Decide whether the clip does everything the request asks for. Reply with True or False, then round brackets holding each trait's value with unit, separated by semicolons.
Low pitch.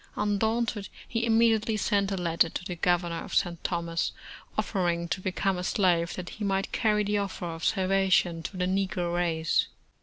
False (185 Hz)